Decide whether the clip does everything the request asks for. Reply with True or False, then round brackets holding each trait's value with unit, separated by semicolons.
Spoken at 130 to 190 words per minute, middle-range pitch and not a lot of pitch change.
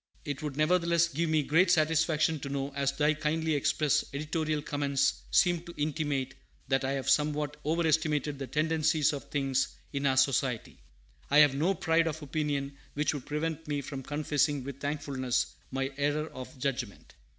True (165 wpm; 150 Hz; 2.3 semitones)